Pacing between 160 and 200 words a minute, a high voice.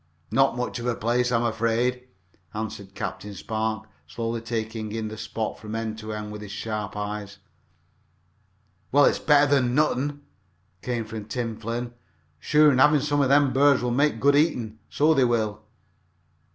No: average, 165 wpm; low, 115 Hz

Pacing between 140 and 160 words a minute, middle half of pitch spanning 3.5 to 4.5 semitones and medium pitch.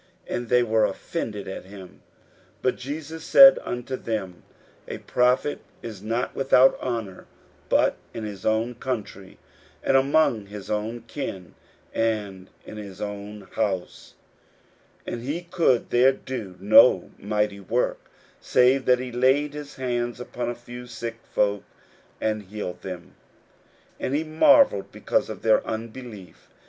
No: average, 145 wpm; average, 3.9 semitones; low, 115 Hz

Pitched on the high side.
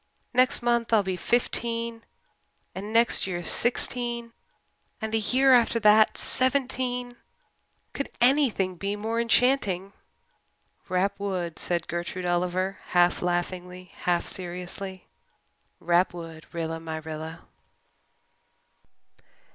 Yes: high, 195 Hz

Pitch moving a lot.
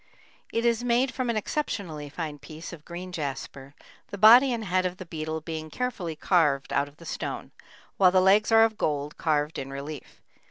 Yes: wide, 6.3 semitones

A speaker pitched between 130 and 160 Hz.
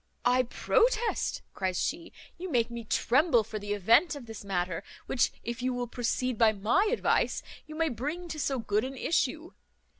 No: high, 245 Hz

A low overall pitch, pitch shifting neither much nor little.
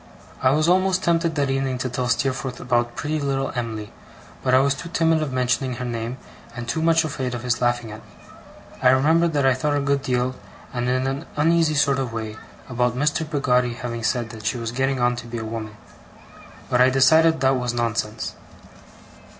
Yes: low, 130 Hz; average, 3.0 semitones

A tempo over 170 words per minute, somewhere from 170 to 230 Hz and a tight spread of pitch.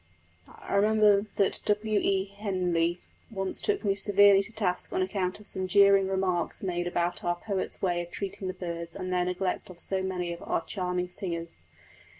Yes: average, 180 wpm; high, 190 Hz; narrow, 2.0 semitones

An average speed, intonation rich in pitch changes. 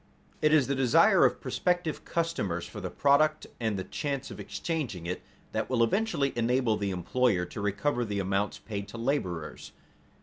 Yes: average, 170 wpm; wide, 6.1 semitones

